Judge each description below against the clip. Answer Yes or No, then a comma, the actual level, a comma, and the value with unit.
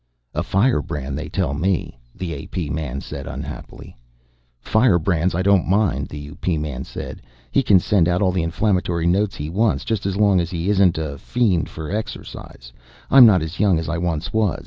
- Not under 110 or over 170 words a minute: No, average, 190 wpm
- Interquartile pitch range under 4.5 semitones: Yes, average, 4.1 semitones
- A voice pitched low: Yes, very low, 90 Hz